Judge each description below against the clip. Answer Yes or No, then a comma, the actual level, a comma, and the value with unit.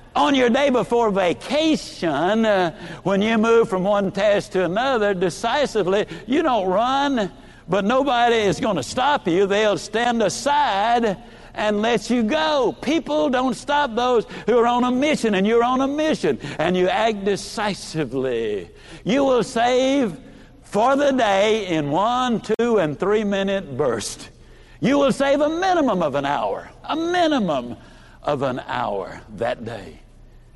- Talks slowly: No, average, 150 wpm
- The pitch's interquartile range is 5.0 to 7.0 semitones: Yes, wide, 5.4 semitones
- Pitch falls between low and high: No, high, 230 Hz